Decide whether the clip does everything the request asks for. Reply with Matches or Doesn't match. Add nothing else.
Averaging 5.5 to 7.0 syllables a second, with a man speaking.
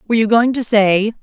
Doesn't match